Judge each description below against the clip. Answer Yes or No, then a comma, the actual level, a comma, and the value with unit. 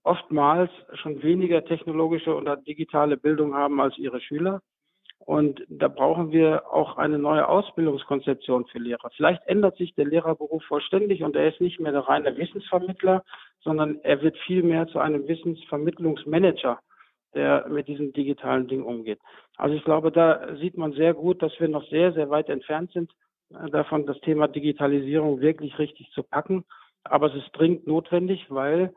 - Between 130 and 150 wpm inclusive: No, average, 160 wpm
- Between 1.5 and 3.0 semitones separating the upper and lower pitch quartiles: Yes, narrow, 2.6 semitones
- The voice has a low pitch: No, medium, 155 Hz